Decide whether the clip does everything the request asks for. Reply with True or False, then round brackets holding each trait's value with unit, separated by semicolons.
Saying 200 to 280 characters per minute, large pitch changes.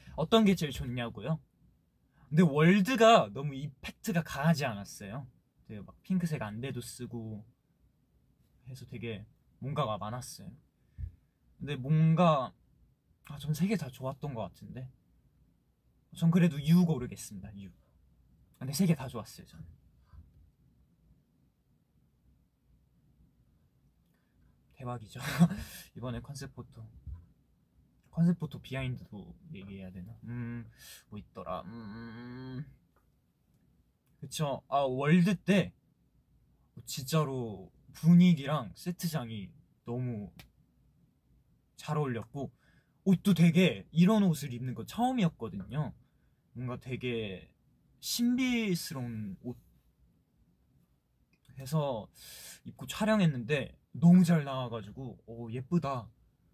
True (205 characters per minute; 5.9 semitones)